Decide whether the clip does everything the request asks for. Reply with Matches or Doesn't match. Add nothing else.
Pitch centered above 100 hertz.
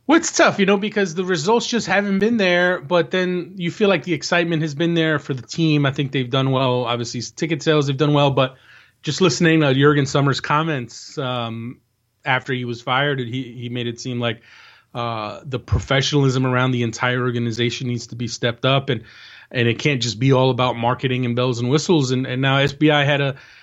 Matches